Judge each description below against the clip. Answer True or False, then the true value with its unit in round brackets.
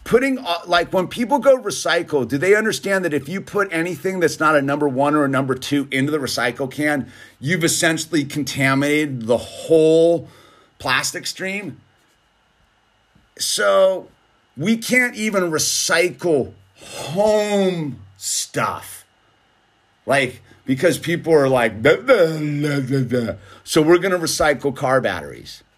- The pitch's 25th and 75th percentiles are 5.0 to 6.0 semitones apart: True (5.5 semitones)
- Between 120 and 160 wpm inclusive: True (135 wpm)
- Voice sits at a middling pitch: True (155 Hz)